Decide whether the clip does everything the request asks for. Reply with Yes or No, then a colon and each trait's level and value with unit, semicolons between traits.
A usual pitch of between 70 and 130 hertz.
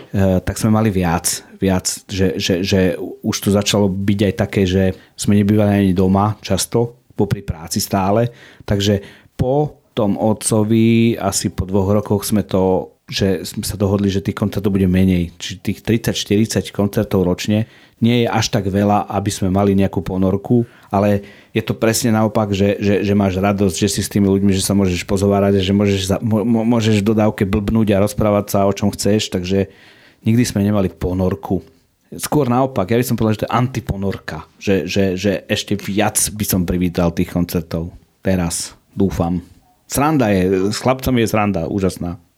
Yes: low, 100 Hz